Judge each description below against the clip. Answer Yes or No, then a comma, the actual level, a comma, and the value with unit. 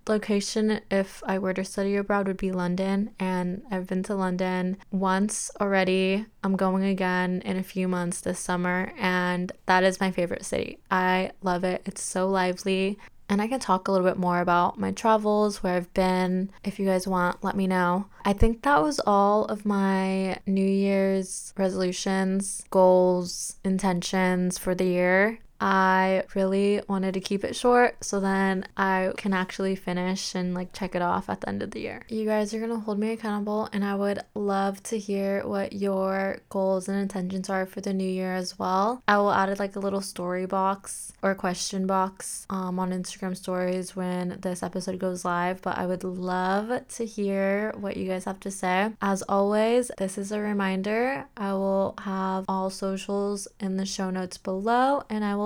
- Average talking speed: Yes, average, 190 wpm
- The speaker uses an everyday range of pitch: No, narrow, 1.3 semitones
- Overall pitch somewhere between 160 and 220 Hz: Yes, high, 190 Hz